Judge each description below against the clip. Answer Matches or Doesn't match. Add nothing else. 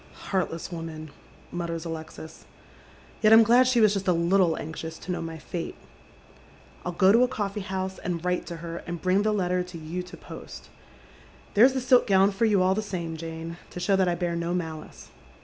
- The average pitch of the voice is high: Doesn't match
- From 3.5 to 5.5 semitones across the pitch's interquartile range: Doesn't match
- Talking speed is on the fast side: Matches